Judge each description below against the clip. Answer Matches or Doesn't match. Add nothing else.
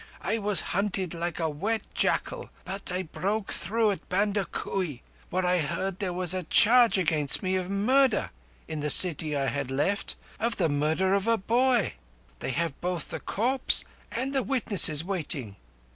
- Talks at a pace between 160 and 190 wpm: Matches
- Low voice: Doesn't match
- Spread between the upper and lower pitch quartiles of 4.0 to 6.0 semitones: Matches